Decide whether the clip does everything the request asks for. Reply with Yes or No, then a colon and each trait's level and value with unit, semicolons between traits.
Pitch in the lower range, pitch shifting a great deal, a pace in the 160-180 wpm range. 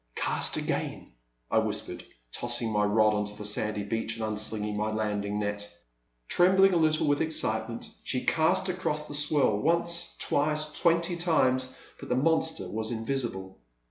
No: low, 120 Hz; wide, 7.0 semitones; average, 150 wpm